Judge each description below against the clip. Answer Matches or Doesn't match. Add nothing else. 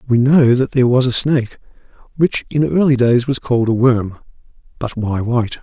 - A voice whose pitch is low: Matches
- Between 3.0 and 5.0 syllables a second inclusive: Doesn't match